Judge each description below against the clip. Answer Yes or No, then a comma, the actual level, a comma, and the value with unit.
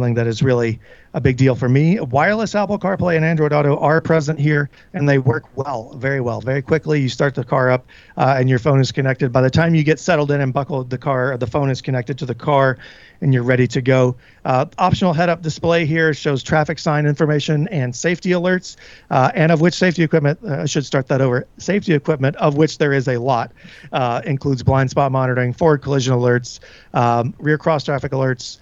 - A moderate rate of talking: No, fast, 220 wpm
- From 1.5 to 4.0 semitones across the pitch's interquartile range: Yes, average, 3.4 semitones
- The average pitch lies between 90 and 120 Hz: No, medium, 140 Hz